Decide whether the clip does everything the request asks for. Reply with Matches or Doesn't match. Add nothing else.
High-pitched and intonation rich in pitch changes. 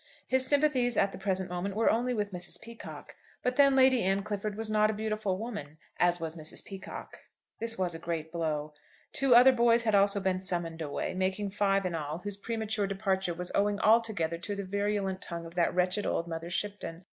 Doesn't match